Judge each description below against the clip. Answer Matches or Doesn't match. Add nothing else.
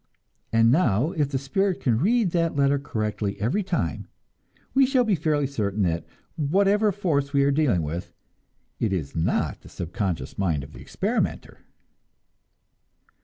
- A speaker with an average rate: Matches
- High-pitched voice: Doesn't match